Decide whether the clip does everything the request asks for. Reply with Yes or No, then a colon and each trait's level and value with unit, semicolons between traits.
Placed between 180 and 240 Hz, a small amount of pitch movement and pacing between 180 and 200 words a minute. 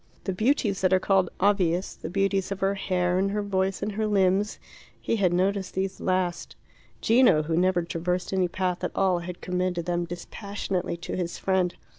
Yes: medium, 185 Hz; narrow, 1.8 semitones; average, 185 wpm